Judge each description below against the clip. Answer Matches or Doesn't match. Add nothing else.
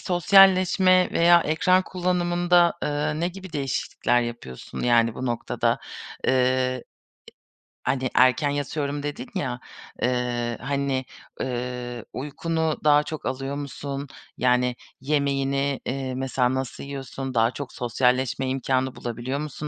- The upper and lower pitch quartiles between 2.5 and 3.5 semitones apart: Matches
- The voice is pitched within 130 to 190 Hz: Matches